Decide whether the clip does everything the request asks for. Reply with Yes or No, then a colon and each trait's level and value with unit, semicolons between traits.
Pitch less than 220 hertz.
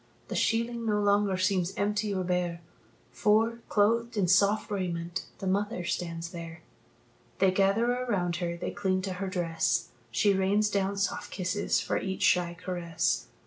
Yes: high, 190 Hz